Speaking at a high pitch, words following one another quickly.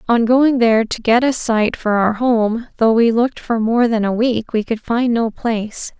Yes: high, 230 Hz; fast, 230 wpm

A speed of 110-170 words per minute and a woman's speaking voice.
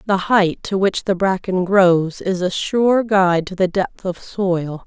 No: average, 195 wpm; female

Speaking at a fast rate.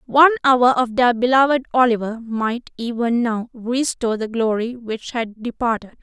No: average, 150 wpm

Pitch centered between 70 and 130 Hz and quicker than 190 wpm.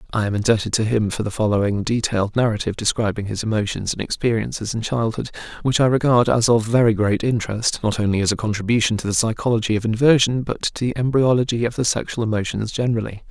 Yes: low, 110 Hz; average, 200 wpm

